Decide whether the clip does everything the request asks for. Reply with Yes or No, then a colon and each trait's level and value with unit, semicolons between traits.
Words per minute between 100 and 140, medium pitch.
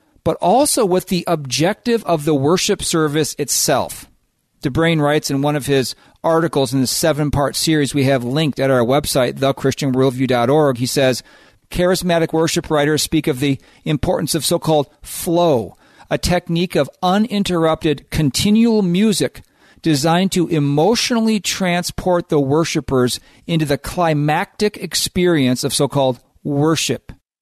Yes: slow, 135 wpm; medium, 155 Hz